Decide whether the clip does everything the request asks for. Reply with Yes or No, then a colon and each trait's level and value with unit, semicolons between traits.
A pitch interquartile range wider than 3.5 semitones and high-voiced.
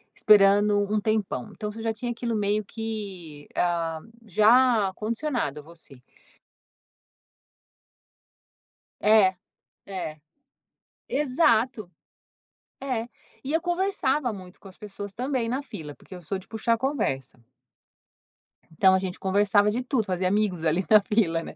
Yes: average, 3.9 semitones; high, 210 Hz